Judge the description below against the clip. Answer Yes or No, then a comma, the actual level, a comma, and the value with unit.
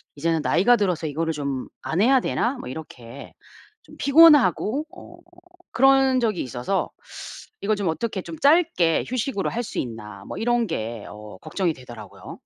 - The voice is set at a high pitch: No, medium, 180 Hz